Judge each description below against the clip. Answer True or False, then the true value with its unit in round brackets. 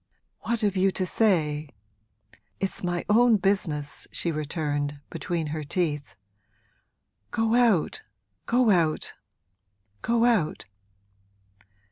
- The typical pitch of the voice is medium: True (180 Hz)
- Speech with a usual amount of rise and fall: False (6.4 semitones)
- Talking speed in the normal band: False (100 wpm)